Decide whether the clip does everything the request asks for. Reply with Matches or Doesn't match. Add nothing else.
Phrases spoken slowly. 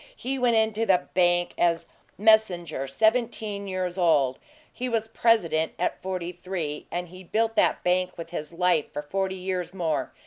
Doesn't match